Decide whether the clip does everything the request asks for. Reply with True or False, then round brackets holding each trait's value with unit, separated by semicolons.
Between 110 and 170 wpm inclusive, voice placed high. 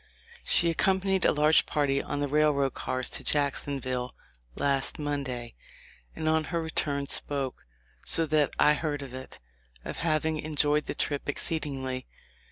False (145 wpm; 145 Hz)